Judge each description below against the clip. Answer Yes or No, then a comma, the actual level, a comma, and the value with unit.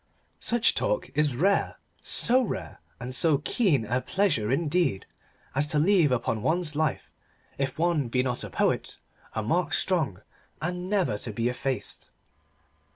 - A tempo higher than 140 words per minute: Yes, average, 150 wpm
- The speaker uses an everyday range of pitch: No, wide, 6.3 semitones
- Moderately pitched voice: Yes, medium, 150 Hz